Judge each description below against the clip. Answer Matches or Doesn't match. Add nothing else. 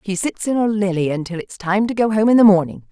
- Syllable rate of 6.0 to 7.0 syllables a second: Matches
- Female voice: Matches